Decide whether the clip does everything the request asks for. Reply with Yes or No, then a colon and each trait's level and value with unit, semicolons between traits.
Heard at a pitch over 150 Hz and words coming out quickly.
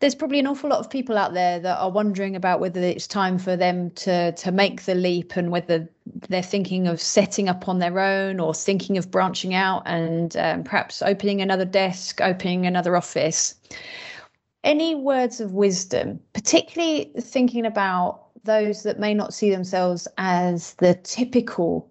No: high, 190 Hz; average, 175 wpm